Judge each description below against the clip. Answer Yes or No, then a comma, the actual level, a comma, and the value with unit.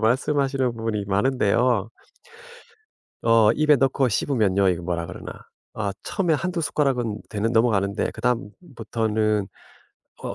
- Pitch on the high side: No, low, 115 Hz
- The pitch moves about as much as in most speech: Yes, average, 4.5 semitones